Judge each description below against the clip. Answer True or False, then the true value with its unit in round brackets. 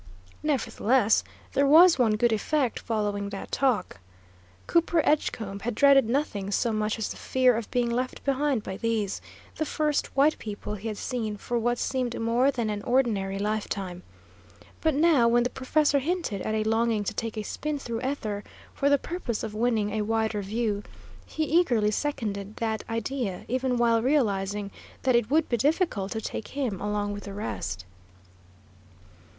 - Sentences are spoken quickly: False (170 wpm)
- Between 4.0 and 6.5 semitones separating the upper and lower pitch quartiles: True (4.3 semitones)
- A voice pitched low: False (230 Hz)